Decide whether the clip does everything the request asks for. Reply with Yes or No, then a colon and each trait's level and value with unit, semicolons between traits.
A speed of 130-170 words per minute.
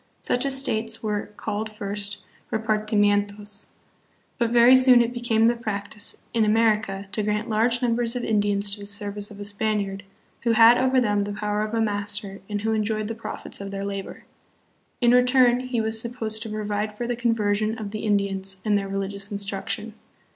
No: average, 185 wpm